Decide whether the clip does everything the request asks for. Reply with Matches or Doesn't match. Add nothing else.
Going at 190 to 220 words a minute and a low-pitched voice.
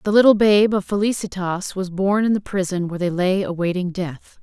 Doesn't match